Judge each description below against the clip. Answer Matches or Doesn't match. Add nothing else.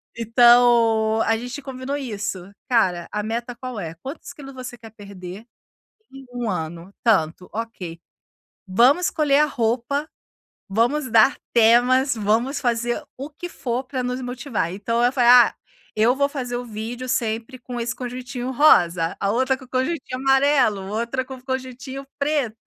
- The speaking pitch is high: Matches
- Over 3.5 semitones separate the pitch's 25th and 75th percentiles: Doesn't match